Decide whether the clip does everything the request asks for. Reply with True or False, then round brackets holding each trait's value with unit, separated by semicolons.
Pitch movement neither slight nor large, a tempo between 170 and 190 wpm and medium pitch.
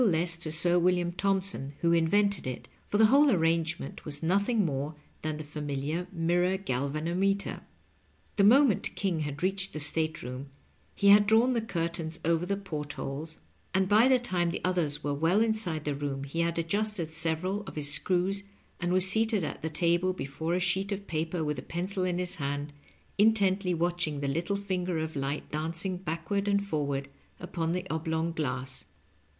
True (3.9 semitones; 180 wpm; 170 Hz)